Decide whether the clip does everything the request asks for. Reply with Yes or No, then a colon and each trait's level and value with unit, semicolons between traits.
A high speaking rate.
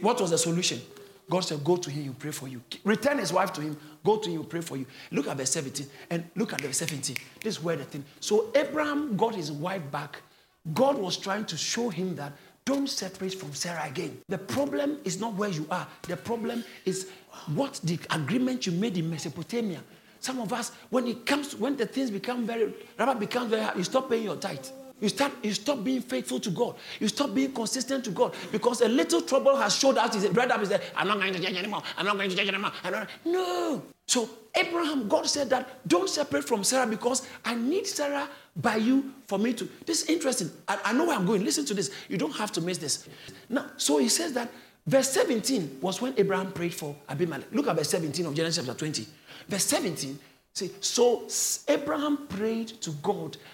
Yes: fast, 225 wpm